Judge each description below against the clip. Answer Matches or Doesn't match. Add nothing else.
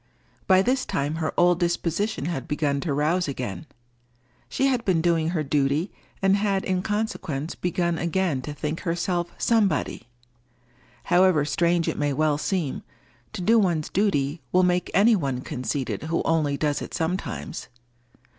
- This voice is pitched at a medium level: Matches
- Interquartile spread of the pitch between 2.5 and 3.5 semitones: Doesn't match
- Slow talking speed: Doesn't match